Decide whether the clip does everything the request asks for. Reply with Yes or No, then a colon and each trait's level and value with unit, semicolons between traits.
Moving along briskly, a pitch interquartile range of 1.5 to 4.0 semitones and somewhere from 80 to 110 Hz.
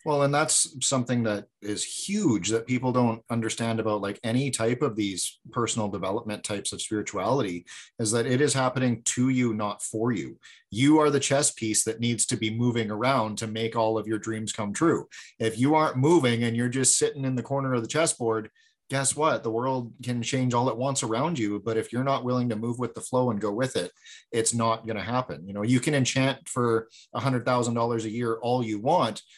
No: fast, 225 wpm; average, 2.8 semitones; low, 120 Hz